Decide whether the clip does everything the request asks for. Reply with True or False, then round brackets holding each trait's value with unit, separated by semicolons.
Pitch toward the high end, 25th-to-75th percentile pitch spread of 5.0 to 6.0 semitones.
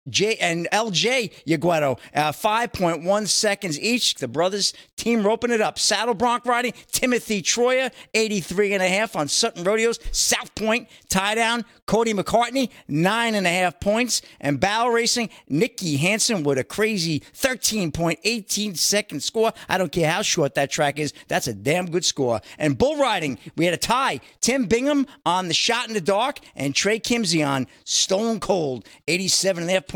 True (205 Hz; 5.4 semitones)